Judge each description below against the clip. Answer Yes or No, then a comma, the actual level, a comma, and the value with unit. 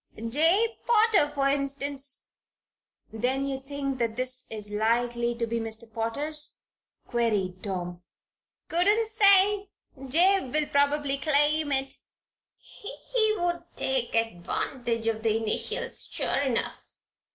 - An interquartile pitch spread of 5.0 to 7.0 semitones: Yes, average, 5.3 semitones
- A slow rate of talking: Yes, slow, 110 wpm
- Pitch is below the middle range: No, very high, 270 Hz